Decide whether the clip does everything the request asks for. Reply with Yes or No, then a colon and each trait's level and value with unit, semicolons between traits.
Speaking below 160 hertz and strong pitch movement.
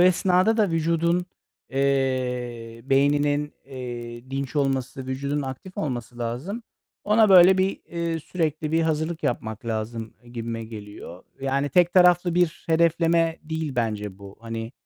Yes: medium, 140 Hz; wide, 5.8 semitones